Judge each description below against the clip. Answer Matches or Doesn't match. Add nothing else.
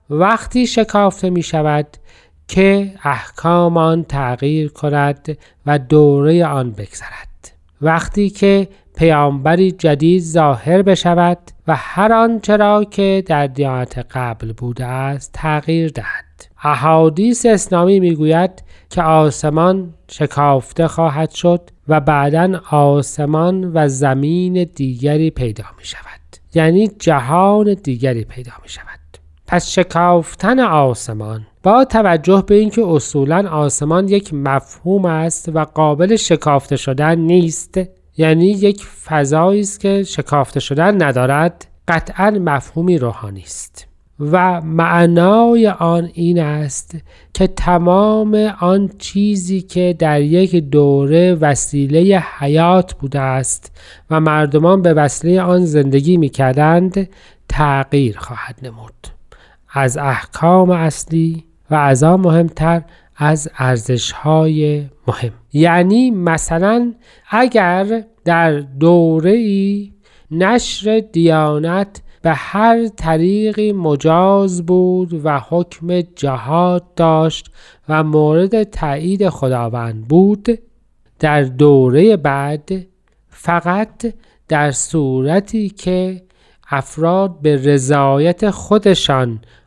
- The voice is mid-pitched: Matches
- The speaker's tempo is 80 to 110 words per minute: Matches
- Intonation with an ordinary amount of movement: Matches